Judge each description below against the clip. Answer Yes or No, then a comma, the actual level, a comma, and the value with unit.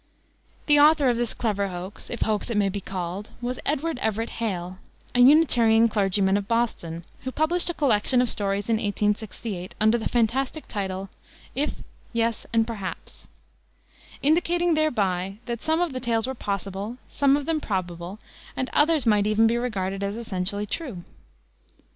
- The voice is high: Yes, high, 225 Hz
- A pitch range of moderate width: Yes, average, 4.6 semitones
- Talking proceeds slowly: No, average, 160 wpm